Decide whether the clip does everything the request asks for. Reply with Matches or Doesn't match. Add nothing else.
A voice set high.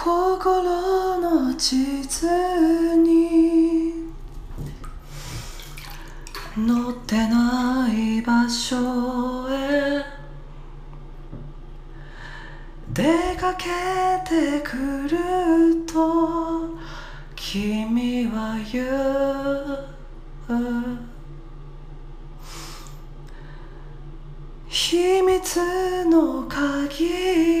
Matches